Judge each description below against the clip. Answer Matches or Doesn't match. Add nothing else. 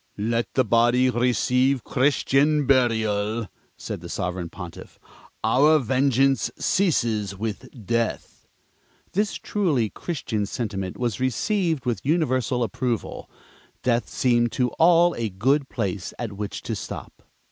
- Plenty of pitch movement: Doesn't match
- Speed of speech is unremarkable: Doesn't match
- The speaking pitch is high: Doesn't match